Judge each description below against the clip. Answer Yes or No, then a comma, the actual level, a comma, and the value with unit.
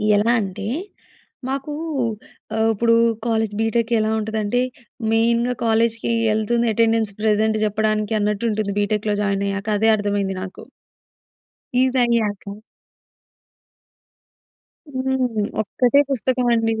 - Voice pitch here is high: Yes, high, 220 Hz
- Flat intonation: Yes, narrow, 2.1 semitones